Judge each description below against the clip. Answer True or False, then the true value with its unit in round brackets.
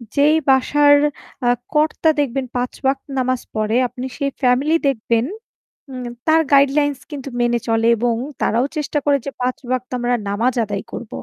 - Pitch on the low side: False (255 Hz)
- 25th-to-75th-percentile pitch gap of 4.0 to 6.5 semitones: False (3.1 semitones)